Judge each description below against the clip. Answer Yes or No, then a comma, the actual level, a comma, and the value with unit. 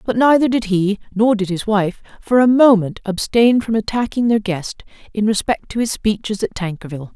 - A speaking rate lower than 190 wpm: No, average, 195 wpm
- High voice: Yes, high, 215 Hz